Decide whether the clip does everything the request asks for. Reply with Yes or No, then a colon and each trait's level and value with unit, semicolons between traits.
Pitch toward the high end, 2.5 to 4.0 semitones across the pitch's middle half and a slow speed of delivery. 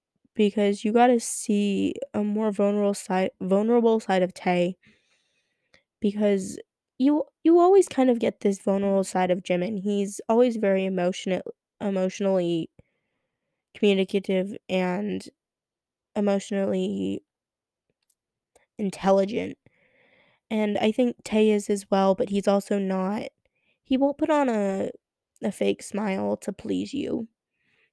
Yes: high, 200 Hz; average, 2.8 semitones; slow, 120 wpm